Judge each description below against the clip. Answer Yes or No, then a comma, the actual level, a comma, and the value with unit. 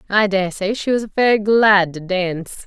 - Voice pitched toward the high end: Yes, high, 200 Hz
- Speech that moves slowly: No, average, 200 wpm